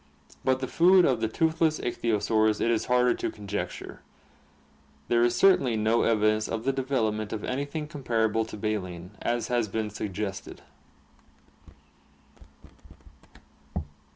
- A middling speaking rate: No, slow, 125 wpm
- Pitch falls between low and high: No, low, 115 Hz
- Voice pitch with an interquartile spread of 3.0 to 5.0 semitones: Yes, average, 3.4 semitones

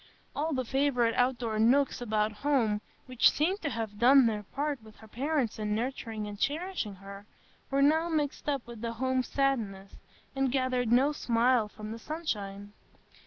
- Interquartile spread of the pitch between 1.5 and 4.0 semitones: No, average, 4.4 semitones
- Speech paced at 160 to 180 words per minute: Yes, average, 165 wpm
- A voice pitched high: Yes, high, 245 Hz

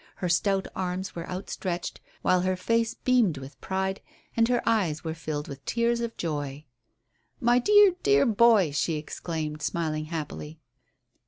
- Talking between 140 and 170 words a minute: Yes, average, 150 wpm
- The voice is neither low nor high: Yes, medium, 180 Hz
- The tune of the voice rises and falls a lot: Yes, wide, 6.8 semitones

